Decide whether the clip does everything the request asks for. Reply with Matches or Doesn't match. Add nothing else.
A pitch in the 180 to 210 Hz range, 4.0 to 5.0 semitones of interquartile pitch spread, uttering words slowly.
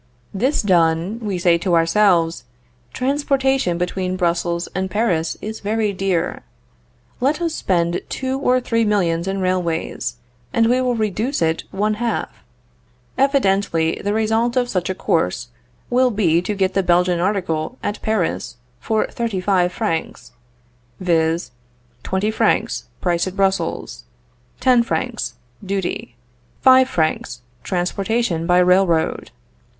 Matches